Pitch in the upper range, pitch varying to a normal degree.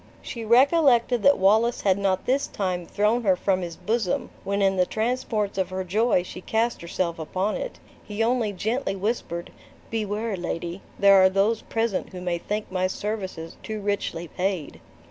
Yes: high, 200 Hz; average, 3.4 semitones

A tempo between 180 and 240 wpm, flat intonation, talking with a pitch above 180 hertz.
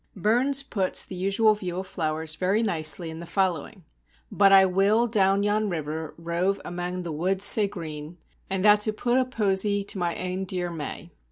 No: average, 185 wpm; average, 3.2 semitones; high, 190 Hz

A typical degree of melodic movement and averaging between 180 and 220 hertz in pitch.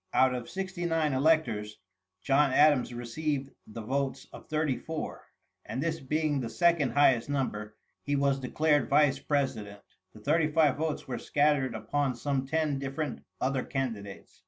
No: average, 3.2 semitones; medium, 140 Hz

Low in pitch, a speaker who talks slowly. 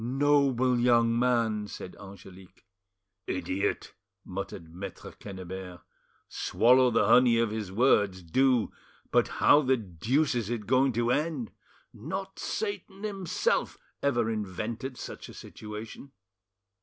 Yes: low, 115 Hz; slow, 120 wpm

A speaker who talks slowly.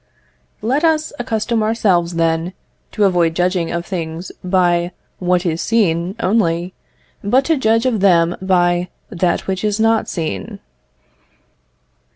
Yes: slow, 130 wpm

